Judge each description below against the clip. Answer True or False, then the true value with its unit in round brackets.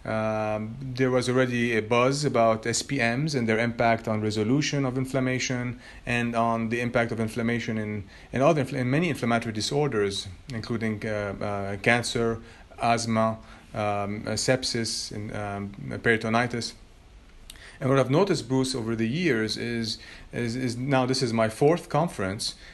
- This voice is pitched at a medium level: False (115 Hz)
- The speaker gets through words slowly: False (145 wpm)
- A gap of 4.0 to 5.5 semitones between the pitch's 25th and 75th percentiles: False (2.8 semitones)